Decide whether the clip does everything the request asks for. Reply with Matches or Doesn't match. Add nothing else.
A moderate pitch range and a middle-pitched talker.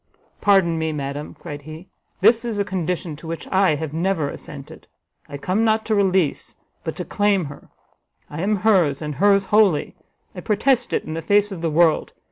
Matches